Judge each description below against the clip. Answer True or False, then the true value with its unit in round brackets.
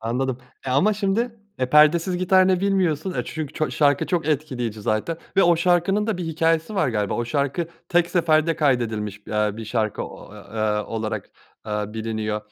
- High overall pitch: False (150 Hz)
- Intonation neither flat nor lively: False (7.9 semitones)